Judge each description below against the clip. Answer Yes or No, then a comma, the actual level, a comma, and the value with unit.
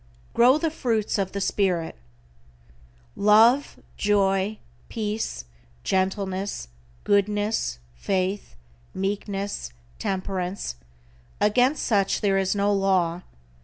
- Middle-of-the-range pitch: No, high, 200 Hz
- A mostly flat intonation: Yes, narrow, 1.8 semitones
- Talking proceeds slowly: Yes, slow, 90 wpm